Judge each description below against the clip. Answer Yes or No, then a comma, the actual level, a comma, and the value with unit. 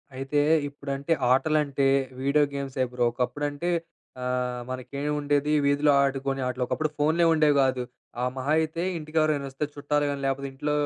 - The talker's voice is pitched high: No, medium, 140 Hz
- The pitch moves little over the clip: Yes, narrow, 1.8 semitones